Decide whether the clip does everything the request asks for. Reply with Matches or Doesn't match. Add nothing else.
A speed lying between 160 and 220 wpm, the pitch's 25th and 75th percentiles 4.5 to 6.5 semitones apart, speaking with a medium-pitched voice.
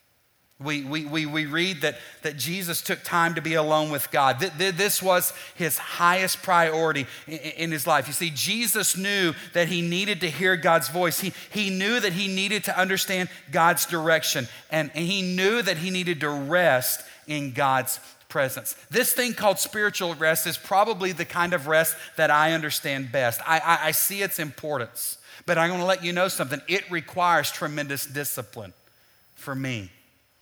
Doesn't match